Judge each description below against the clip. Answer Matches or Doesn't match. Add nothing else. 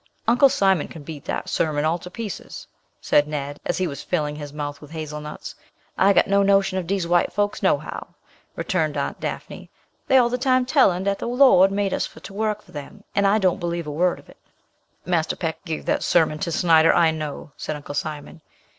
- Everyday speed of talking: Doesn't match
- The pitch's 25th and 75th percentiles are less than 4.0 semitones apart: Doesn't match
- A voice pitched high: Doesn't match